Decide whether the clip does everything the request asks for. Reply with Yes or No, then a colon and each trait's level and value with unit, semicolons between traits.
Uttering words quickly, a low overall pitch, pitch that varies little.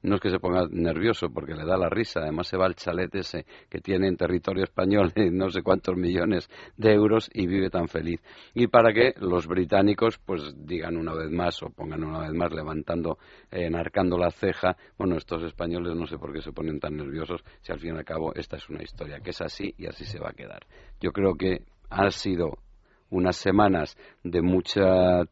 Yes: fast, 215 wpm; very low, 90 Hz; narrow, 2.3 semitones